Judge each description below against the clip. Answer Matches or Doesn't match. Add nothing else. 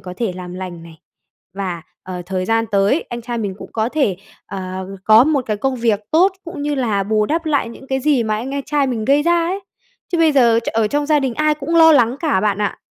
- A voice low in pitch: Doesn't match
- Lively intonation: Matches